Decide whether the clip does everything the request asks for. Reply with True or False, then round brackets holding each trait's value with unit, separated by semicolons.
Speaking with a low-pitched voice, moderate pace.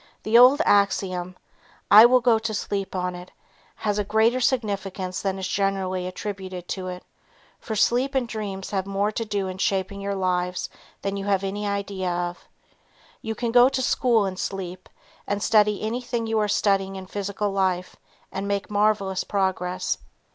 False (200 Hz; 170 wpm)